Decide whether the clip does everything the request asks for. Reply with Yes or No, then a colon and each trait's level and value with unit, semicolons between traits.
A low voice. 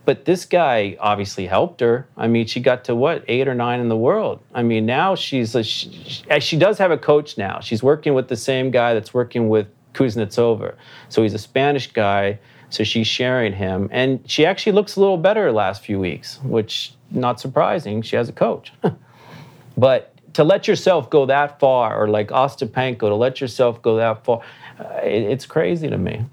Yes: low, 120 Hz